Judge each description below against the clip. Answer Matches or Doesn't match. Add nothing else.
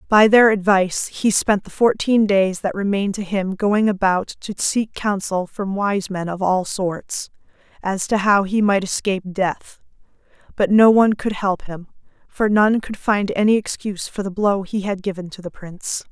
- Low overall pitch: Doesn't match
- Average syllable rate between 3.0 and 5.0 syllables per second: Matches